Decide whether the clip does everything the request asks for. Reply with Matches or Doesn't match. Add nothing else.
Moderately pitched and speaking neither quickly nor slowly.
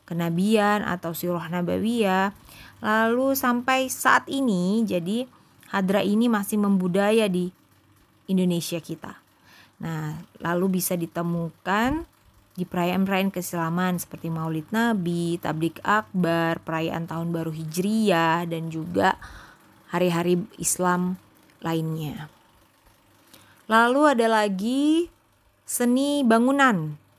Matches